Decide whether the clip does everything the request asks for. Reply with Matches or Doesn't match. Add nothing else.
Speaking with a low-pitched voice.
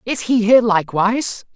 Doesn't match